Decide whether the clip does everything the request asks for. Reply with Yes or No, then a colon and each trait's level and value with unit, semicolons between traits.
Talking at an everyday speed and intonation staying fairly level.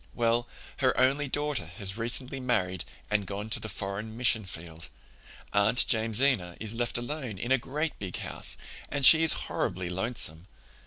No: average, 160 wpm; average, 4.6 semitones